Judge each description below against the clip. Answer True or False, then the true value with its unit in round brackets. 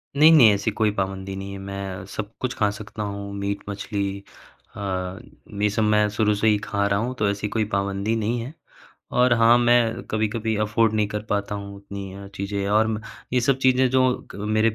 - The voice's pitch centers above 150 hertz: False (105 Hz)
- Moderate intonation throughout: False (2.2 semitones)